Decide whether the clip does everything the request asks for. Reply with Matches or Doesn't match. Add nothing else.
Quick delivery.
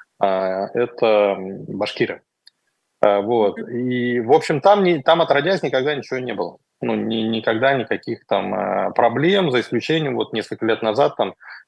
Doesn't match